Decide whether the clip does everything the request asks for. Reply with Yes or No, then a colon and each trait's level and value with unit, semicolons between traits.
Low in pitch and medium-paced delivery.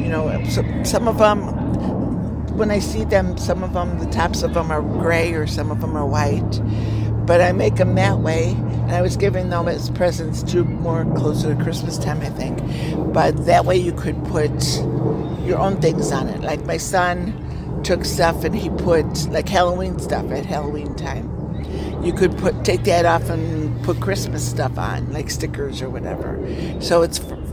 Yes: low, 105 Hz; average, 190 wpm